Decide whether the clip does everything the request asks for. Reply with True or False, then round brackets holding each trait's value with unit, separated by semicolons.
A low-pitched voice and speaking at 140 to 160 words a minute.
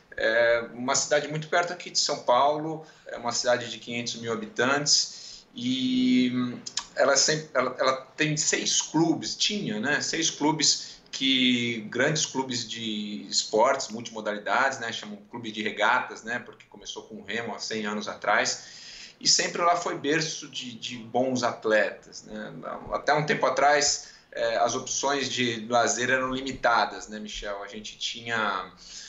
True (130 Hz; 155 wpm)